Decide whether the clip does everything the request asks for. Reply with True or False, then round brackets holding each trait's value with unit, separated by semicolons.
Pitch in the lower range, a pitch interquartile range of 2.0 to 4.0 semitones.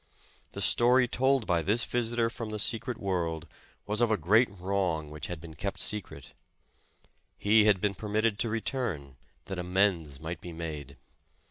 False (100 Hz; 5.3 semitones)